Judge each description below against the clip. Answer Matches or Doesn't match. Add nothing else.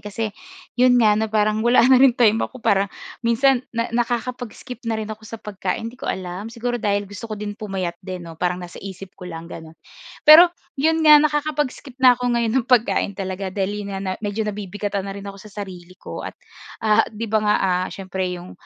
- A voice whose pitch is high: Matches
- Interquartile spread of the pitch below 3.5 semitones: Doesn't match